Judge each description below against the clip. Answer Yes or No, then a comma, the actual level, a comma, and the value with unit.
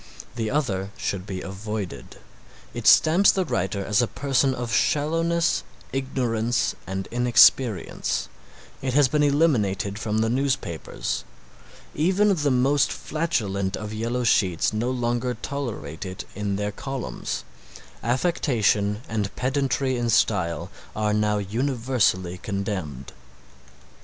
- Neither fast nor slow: No, slow, 115 wpm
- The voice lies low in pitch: Yes, low, 115 Hz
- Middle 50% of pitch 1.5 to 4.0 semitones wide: No, average, 5.3 semitones